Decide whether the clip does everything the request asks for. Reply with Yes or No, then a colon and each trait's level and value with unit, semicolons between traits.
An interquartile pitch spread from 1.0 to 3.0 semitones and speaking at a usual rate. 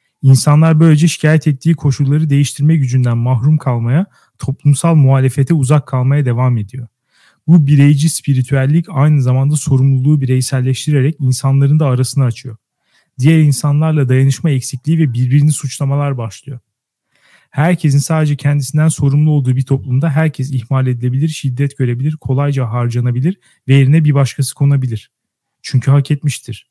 Yes: narrow, 2.5 semitones; average, 125 wpm